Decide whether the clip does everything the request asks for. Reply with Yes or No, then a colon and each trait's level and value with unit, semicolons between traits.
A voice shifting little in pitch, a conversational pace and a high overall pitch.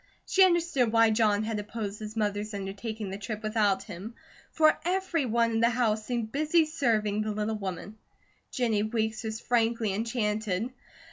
Yes: narrow, 2.1 semitones; average, 155 wpm; high, 220 Hz